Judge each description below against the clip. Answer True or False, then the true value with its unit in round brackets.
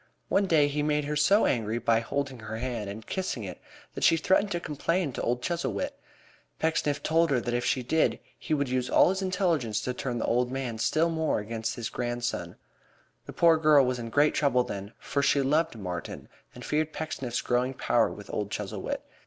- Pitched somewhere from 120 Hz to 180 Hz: True (135 Hz)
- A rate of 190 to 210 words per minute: True (200 wpm)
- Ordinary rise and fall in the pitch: True (4.9 semitones)